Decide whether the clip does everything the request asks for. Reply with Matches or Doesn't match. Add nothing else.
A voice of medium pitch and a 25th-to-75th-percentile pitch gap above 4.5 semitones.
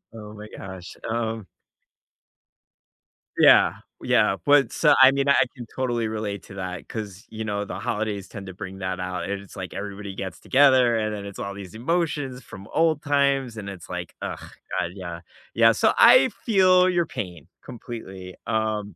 Doesn't match